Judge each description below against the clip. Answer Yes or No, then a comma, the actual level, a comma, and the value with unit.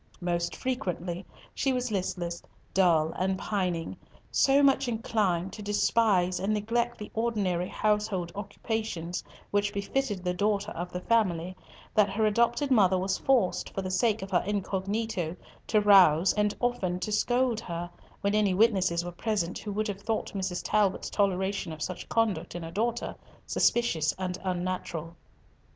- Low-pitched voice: No, high, 195 Hz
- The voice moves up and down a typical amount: Yes, average, 3.5 semitones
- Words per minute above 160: No, average, 155 wpm